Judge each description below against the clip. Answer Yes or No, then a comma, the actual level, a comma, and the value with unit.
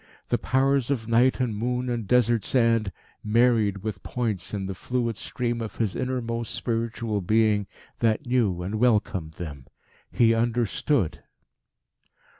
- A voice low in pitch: Yes, low, 115 Hz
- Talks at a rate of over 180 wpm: No, slow, 135 wpm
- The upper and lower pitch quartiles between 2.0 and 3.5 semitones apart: Yes, average, 2.9 semitones